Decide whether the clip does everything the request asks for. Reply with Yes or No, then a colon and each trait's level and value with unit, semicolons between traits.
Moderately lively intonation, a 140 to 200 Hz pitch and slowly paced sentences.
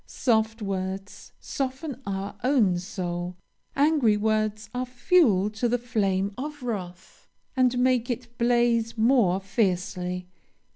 No: average, 4.4 semitones; high, 220 Hz; slow, 115 wpm